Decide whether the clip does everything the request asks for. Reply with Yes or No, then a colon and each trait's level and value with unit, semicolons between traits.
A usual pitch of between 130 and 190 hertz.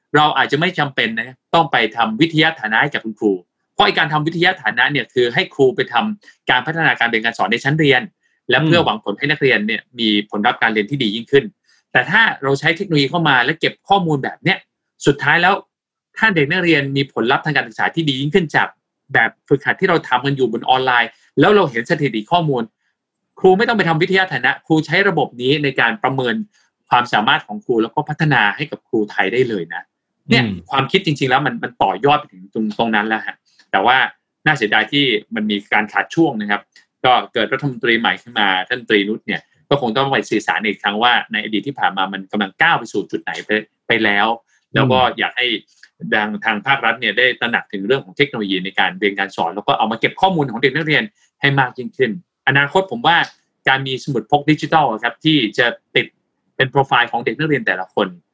Yes: low, 135 Hz